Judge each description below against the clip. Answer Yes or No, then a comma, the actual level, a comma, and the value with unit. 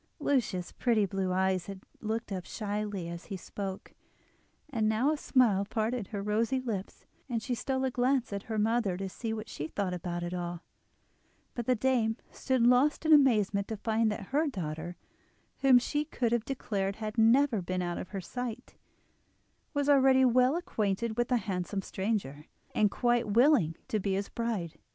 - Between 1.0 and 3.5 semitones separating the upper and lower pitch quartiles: No, average, 4.4 semitones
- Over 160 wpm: Yes, average, 180 wpm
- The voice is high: Yes, high, 220 Hz